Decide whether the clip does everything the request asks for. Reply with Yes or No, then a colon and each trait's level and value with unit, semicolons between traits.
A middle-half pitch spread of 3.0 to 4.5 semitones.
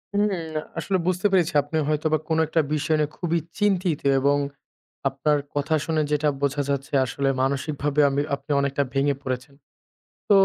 No: narrow, 2.6 semitones